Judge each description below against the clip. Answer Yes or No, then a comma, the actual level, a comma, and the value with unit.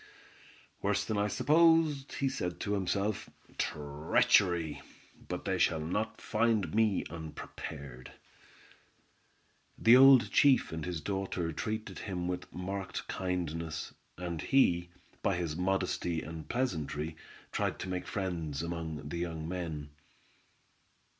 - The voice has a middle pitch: No, very low, 90 Hz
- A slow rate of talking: Yes, slow, 120 wpm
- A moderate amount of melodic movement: Yes, average, 4.2 semitones